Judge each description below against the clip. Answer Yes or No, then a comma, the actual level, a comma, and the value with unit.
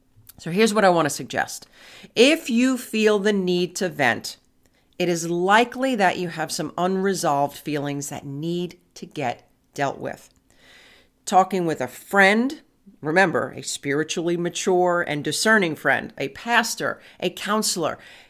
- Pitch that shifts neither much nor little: No, wide, 5.8 semitones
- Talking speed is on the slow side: No, average, 145 wpm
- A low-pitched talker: No, medium, 180 Hz